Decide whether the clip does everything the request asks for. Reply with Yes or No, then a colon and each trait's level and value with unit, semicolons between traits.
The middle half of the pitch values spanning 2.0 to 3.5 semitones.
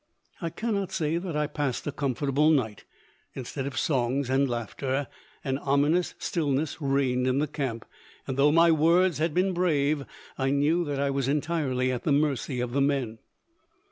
Yes: average, 2.9 semitones